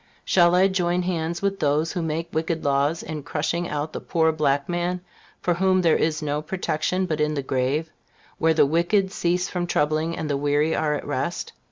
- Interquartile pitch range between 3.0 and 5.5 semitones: No, narrow, 2.6 semitones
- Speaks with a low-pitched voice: No, medium, 160 Hz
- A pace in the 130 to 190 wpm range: No, average, 200 wpm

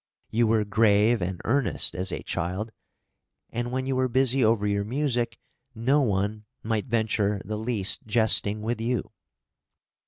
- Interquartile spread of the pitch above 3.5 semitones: No, average, 2.7 semitones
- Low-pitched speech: Yes, low, 110 Hz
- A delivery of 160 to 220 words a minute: No, average, 150 wpm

